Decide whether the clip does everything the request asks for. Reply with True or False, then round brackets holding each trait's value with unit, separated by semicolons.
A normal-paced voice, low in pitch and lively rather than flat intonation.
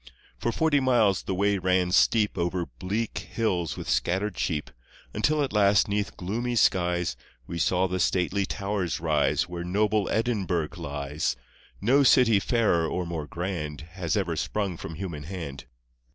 False (155 wpm; 95 Hz; 3.6 semitones)